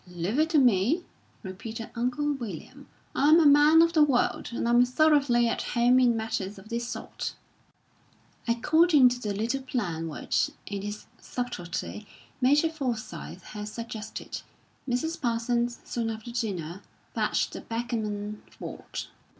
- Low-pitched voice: No, high, 235 Hz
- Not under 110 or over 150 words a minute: Yes, average, 140 wpm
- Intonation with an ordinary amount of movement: Yes, average, 4.2 semitones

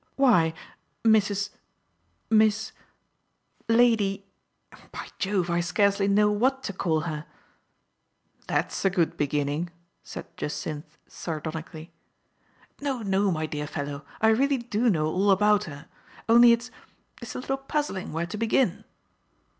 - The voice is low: No, high, 200 Hz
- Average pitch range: No, wide, 5.8 semitones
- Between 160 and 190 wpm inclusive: No, average, 145 wpm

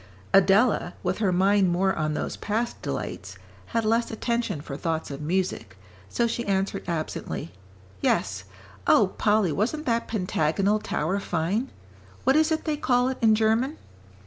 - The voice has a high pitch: Yes, high, 200 Hz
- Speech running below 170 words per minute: Yes, average, 150 wpm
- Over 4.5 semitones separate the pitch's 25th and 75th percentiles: Yes, average, 4.9 semitones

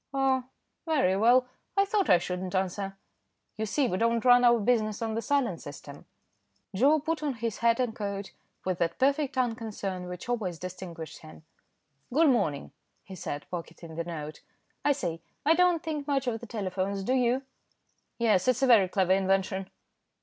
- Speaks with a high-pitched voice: Yes, high, 215 Hz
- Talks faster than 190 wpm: No, average, 170 wpm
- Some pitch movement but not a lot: No, wide, 5.7 semitones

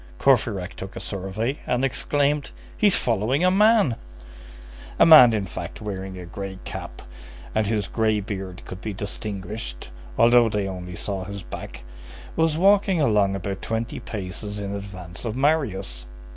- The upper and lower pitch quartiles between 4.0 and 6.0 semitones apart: Yes, average, 4.9 semitones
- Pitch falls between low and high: No, low, 105 Hz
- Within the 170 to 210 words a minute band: No, average, 150 wpm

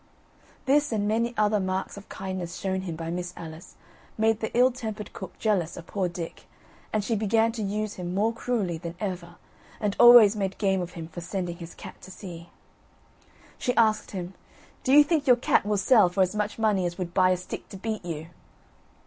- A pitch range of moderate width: Yes, average, 3.6 semitones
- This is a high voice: Yes, high, 195 Hz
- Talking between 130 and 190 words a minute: No, fast, 205 wpm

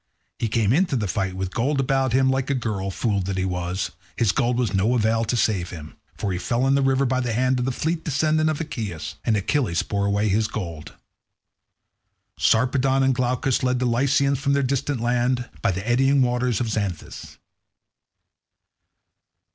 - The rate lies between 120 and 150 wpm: No, average, 195 wpm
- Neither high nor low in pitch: No, low, 120 Hz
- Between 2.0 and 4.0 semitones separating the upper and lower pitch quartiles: No, average, 4.8 semitones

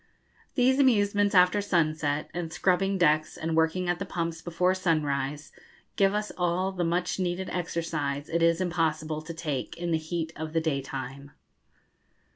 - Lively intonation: No, average, 2.8 semitones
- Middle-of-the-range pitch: Yes, medium, 170 Hz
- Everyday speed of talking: Yes, average, 155 wpm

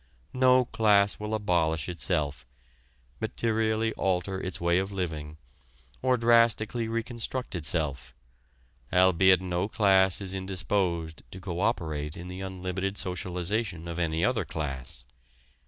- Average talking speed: No, slow, 120 wpm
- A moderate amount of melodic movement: Yes, average, 4.2 semitones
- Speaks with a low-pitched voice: Yes, very low, 95 Hz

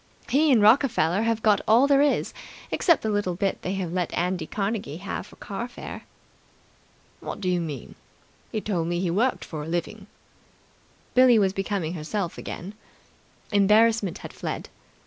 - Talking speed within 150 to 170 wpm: Yes, average, 165 wpm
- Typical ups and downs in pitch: Yes, average, 4.1 semitones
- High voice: Yes, high, 200 Hz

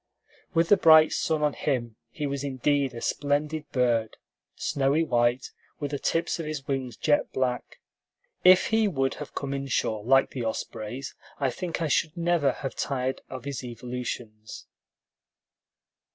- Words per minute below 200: Yes, average, 150 wpm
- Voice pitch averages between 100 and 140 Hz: Yes, low, 135 Hz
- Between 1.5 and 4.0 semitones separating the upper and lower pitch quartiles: Yes, average, 3.5 semitones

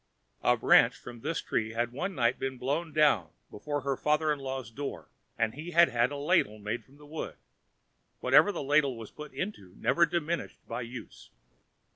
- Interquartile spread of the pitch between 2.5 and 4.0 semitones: No, average, 4.4 semitones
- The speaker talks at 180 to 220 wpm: Yes, average, 185 wpm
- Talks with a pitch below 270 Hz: Yes, medium, 140 Hz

